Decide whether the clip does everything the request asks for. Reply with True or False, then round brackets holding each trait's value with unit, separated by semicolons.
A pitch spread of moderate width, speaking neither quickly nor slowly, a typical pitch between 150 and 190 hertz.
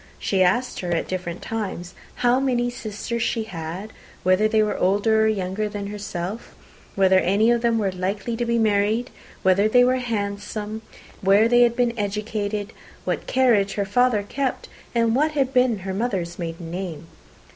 False (3.5 semitones; 170 wpm; 210 Hz)